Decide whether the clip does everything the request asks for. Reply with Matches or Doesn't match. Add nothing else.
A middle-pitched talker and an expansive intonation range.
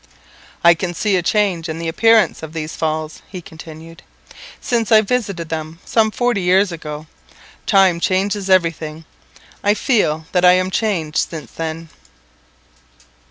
Doesn't match